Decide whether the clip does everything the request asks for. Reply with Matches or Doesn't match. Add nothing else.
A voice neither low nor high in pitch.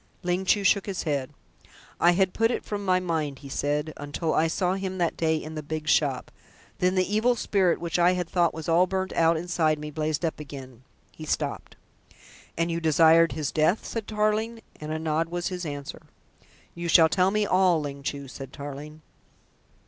Matches